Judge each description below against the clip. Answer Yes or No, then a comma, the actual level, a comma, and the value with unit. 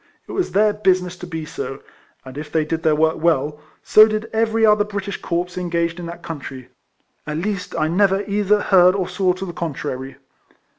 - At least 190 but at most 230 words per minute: Yes, average, 195 wpm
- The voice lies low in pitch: No, medium, 180 Hz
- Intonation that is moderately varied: Yes, average, 4.2 semitones